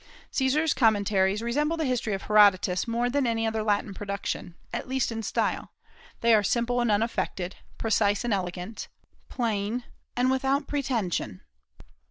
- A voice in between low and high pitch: No, high, 225 Hz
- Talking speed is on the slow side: No, average, 145 wpm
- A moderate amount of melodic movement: Yes, average, 3.7 semitones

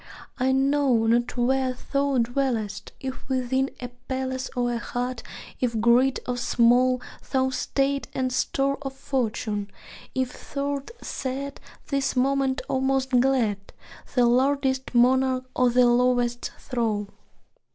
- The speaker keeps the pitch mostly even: Yes, narrow, 1.7 semitones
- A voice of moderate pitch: No, very high, 255 Hz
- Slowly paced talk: Yes, slow, 130 wpm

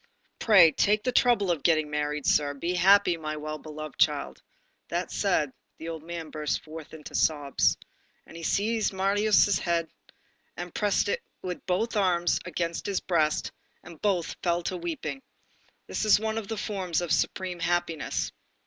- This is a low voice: No, medium, 175 Hz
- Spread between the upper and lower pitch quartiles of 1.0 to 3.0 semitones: No, average, 4.1 semitones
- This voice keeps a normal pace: Yes, average, 165 wpm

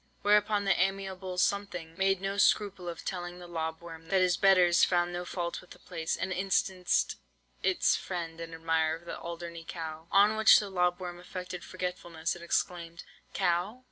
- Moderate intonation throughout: No, narrow, 2.3 semitones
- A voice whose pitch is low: No, medium, 180 Hz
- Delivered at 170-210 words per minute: Yes, average, 175 wpm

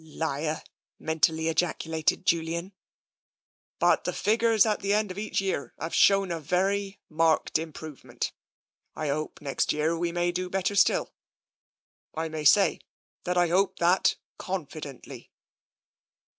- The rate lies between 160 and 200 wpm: No, slow, 135 wpm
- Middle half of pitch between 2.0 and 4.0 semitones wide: Yes, average, 3.4 semitones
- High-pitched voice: No, medium, 170 Hz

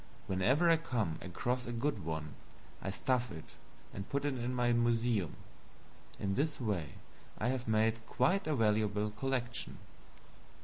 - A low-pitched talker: Yes, low, 120 Hz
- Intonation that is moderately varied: Yes, average, 3.8 semitones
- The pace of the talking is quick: No, average, 145 wpm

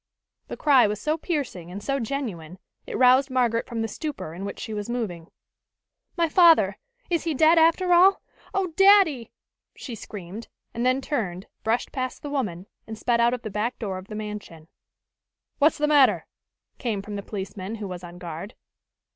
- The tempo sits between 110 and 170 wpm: No, average, 180 wpm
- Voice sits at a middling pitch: No, high, 235 Hz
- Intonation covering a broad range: Yes, wide, 6.4 semitones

